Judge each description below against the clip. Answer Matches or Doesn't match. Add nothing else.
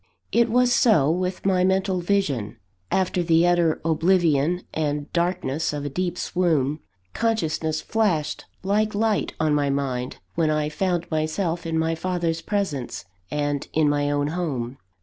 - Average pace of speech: Matches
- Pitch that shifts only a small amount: Doesn't match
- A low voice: Doesn't match